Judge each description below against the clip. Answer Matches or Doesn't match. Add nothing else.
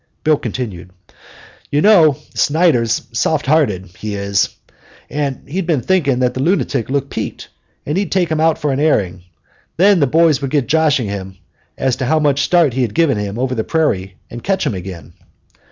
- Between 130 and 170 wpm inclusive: Doesn't match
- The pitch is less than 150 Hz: Matches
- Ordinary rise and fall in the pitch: Doesn't match